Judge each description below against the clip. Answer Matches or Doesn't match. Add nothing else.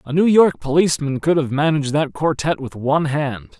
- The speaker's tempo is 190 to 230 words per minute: Matches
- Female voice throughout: Doesn't match